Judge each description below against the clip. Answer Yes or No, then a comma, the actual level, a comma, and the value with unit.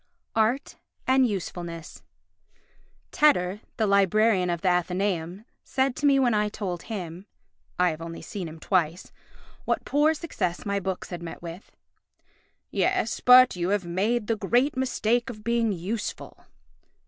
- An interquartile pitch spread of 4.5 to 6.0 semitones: Yes, average, 5.0 semitones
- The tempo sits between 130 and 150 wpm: Yes, average, 145 wpm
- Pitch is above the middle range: Yes, high, 200 Hz